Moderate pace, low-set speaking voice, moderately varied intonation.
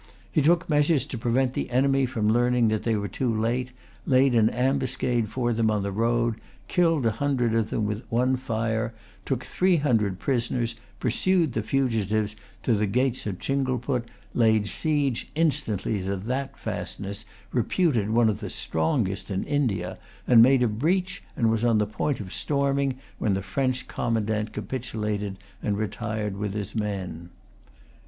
Yes: average, 160 wpm; low, 115 Hz; average, 3.7 semitones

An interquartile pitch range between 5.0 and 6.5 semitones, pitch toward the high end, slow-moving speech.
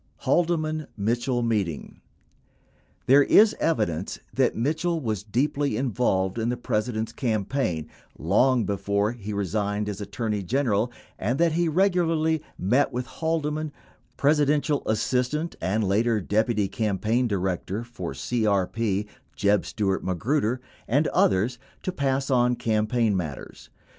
No: wide, 5.6 semitones; low, 115 Hz; slow, 125 wpm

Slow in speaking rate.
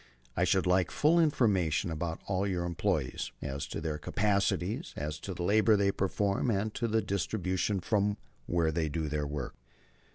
No: average, 175 wpm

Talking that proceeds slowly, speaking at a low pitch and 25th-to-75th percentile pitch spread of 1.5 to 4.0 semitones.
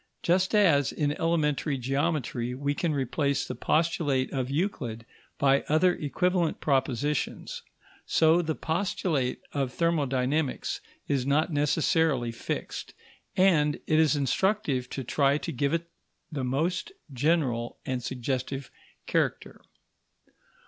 No: slow, 115 wpm; medium, 145 Hz; average, 3.7 semitones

